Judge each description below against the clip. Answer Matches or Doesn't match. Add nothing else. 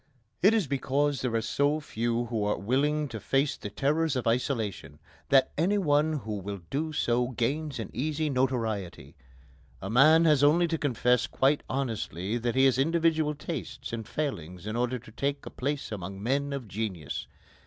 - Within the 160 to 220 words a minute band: Matches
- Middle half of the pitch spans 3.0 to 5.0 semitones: Matches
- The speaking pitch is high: Doesn't match